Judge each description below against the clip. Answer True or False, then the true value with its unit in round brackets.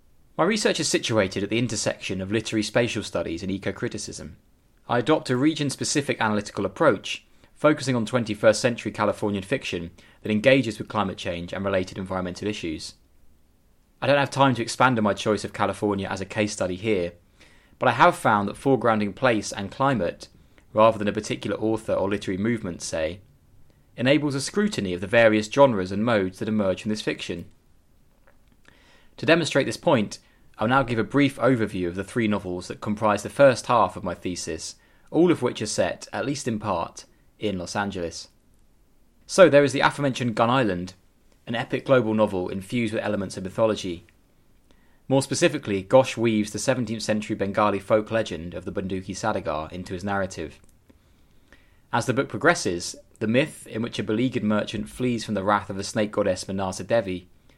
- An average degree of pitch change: True (4.2 semitones)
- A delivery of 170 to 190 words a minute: True (180 wpm)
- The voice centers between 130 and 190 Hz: False (105 Hz)